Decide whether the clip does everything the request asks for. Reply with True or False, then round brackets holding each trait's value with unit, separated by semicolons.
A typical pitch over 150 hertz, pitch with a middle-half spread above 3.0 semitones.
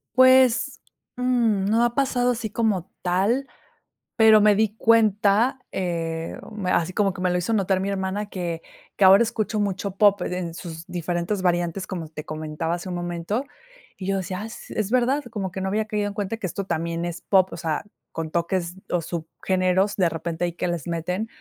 True (190 Hz; 3.8 semitones)